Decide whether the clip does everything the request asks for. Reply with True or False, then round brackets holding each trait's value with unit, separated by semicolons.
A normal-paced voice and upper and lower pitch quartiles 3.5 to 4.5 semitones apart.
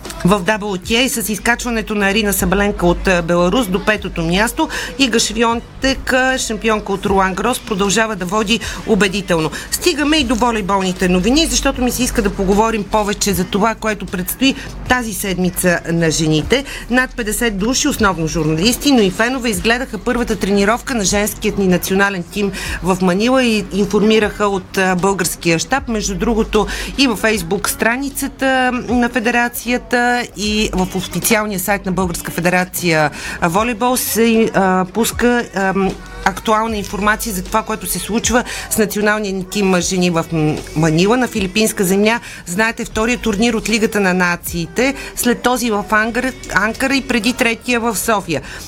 True (145 wpm; 3.9 semitones)